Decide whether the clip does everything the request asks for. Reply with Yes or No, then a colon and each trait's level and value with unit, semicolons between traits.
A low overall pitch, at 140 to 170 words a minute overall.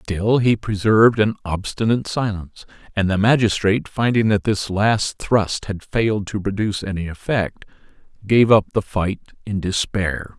Yes: low, 105 Hz; average, 150 wpm